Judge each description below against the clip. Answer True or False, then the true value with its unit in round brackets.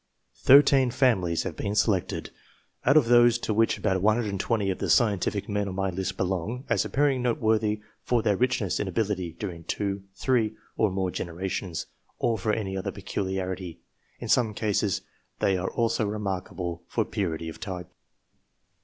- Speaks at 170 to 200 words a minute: False (155 wpm)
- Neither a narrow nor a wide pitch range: True (3.4 semitones)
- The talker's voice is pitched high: False (100 Hz)